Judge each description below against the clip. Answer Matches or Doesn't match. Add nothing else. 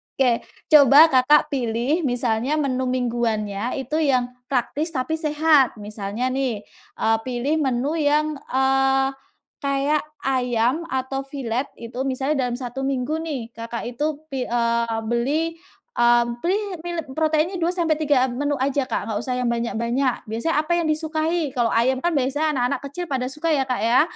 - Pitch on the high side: Matches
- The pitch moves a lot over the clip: Doesn't match